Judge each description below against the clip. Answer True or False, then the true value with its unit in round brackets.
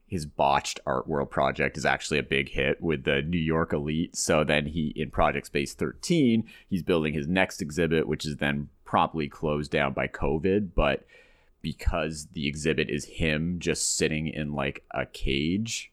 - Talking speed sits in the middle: True (175 wpm)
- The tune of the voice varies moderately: False (2.0 semitones)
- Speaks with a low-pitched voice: True (75 Hz)